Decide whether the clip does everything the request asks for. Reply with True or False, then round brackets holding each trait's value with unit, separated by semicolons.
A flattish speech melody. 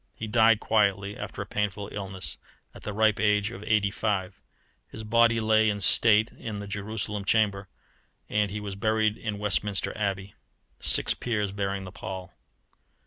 True (1.6 semitones)